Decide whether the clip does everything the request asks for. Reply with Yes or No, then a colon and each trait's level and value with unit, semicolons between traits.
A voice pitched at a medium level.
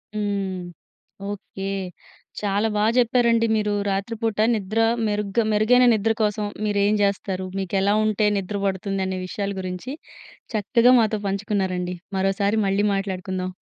No: high, 200 Hz